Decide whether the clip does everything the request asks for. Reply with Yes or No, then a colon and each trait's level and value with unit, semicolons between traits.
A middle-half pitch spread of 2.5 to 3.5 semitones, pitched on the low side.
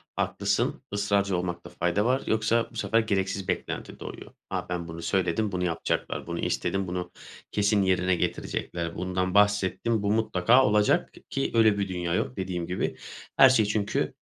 Yes: average, 2.9 semitones; very low, 95 Hz